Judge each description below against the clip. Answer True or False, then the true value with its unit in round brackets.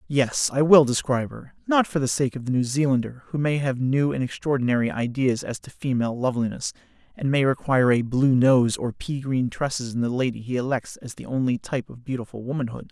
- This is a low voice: True (130 Hz)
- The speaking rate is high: True (215 wpm)